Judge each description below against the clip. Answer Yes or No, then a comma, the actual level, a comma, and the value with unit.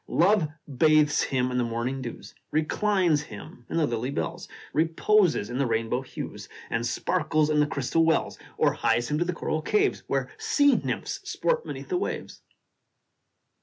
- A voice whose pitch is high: No, medium, 155 Hz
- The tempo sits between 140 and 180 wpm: Yes, average, 165 wpm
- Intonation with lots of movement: Yes, wide, 5.8 semitones